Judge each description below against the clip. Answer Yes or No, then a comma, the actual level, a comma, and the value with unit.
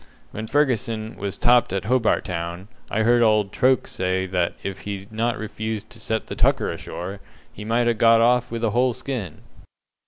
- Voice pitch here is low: Yes, low, 110 Hz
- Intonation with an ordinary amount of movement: Yes, average, 3.3 semitones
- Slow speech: No, average, 185 wpm